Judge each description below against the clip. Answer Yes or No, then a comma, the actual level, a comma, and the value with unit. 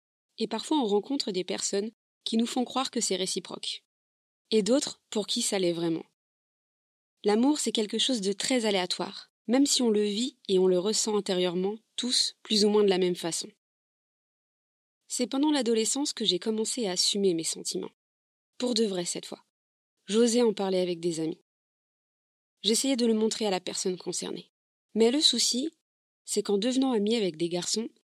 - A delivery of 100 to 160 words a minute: No, average, 180 wpm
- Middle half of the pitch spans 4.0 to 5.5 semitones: Yes, average, 4.3 semitones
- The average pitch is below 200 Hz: No, high, 215 Hz